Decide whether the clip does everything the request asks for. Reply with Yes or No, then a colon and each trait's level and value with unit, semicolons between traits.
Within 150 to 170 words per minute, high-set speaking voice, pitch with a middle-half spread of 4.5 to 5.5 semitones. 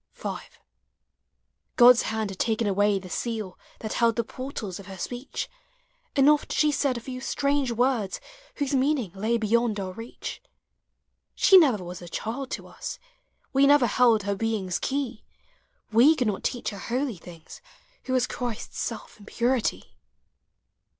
No: average, 155 wpm; high, 235 Hz; average, 4.1 semitones